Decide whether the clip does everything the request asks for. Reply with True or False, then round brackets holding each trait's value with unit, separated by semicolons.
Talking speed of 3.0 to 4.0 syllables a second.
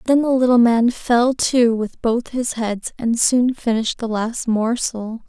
True (3.9 syllables/s)